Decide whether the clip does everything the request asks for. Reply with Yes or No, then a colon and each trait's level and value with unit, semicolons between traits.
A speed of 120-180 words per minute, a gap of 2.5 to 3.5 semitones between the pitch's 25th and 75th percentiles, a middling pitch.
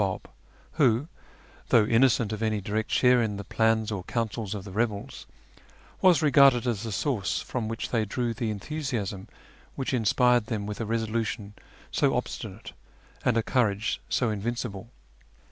No: average, 160 wpm; average, 2.8 semitones; low, 110 Hz